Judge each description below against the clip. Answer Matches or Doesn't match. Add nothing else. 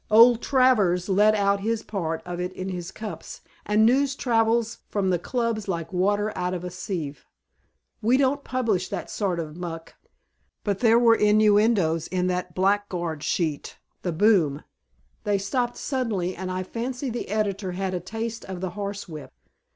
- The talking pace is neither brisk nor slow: Matches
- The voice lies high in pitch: Matches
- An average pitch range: Matches